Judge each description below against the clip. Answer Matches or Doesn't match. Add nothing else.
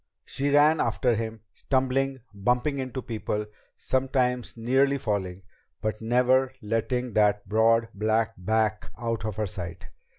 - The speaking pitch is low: Matches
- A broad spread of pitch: Doesn't match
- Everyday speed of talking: Doesn't match